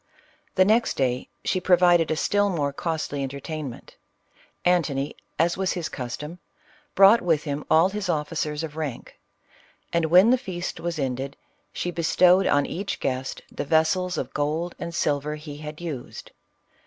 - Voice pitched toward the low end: No, medium, 160 Hz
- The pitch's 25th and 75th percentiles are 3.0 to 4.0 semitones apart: Yes, average, 3.6 semitones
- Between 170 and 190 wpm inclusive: No, average, 155 wpm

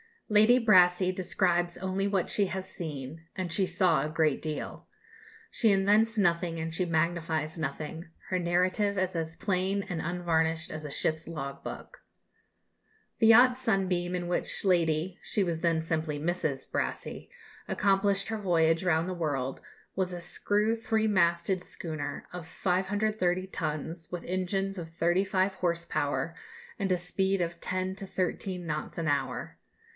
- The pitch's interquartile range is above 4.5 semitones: No, average, 2.9 semitones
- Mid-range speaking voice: Yes, medium, 180 Hz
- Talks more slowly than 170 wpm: Yes, average, 155 wpm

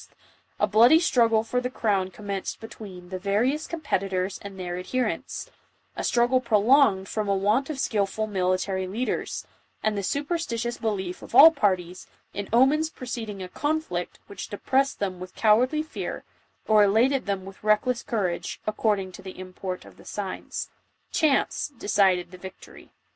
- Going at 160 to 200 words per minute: Yes, average, 165 wpm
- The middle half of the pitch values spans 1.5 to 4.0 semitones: No, average, 4.8 semitones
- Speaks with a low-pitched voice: No, high, 210 Hz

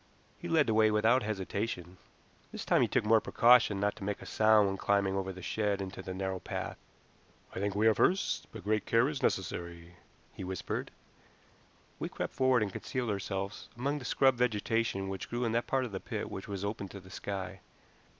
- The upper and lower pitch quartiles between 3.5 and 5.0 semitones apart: No, average, 3.1 semitones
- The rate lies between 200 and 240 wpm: Yes, fast, 205 wpm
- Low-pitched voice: Yes, low, 105 Hz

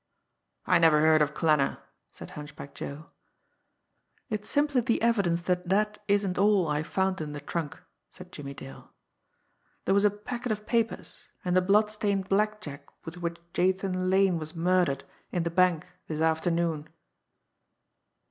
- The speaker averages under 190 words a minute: Yes, average, 150 wpm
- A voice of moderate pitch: Yes, medium, 180 Hz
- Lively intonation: No, average, 4.3 semitones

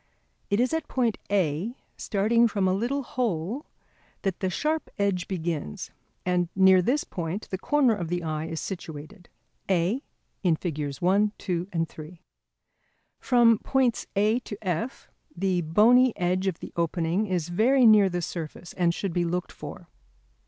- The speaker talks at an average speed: Yes, average, 150 wpm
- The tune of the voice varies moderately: Yes, average, 4.8 semitones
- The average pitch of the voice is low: No, high, 190 Hz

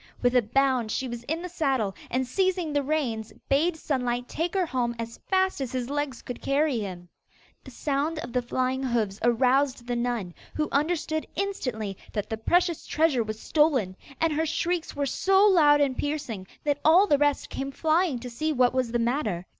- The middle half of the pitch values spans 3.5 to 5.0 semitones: Yes, average, 4.7 semitones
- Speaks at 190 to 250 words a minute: Yes, average, 195 wpm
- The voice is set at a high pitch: Yes, very high, 270 Hz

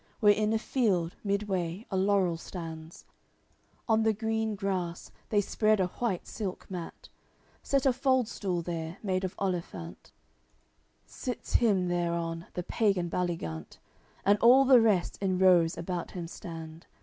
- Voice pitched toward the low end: No, medium, 185 Hz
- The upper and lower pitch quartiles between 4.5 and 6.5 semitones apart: No, average, 4.0 semitones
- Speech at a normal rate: Yes, average, 145 wpm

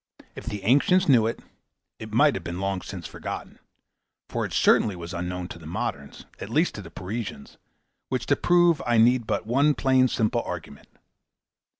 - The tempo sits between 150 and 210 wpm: Yes, average, 185 wpm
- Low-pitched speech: Yes, low, 115 Hz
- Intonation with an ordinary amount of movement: No, wide, 5.7 semitones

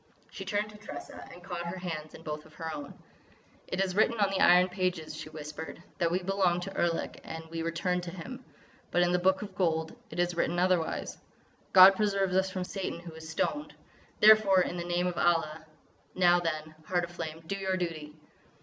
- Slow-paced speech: No, fast, 205 wpm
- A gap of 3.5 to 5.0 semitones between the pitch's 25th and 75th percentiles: No, narrow, 2.5 semitones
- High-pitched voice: No, medium, 175 Hz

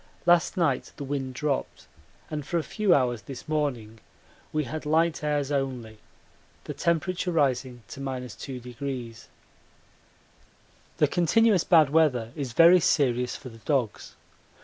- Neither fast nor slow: No, slow, 130 wpm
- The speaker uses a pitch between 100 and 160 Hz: Yes, medium, 140 Hz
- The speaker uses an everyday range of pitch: Yes, average, 4.2 semitones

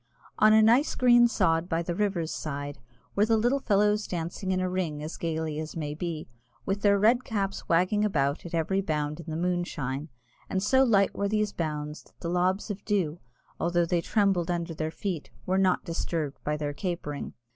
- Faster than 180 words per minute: Yes, average, 195 wpm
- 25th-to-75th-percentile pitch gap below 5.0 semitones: Yes, average, 4.2 semitones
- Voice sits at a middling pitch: Yes, medium, 175 Hz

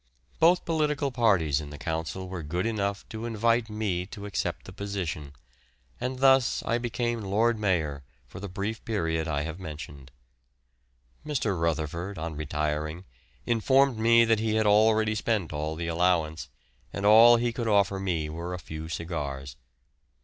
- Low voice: Yes, low, 100 Hz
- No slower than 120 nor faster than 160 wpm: Yes, average, 155 wpm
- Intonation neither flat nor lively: No, wide, 6.0 semitones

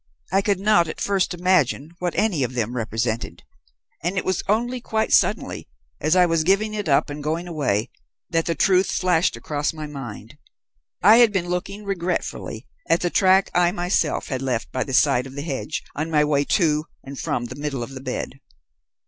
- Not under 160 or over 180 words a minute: No, average, 195 wpm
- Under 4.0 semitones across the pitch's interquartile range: No, average, 5.3 semitones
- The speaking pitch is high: No, medium, 165 Hz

